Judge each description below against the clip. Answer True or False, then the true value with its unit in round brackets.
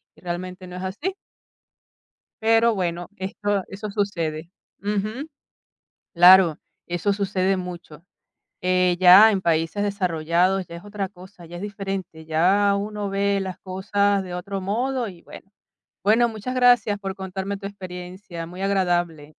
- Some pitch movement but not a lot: False (2.3 semitones)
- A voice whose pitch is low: False (190 Hz)